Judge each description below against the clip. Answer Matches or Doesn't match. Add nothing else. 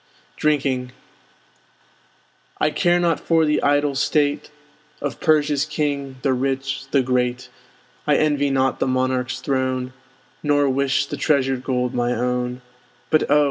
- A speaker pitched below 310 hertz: Matches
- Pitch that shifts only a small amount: Matches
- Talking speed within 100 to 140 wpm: Matches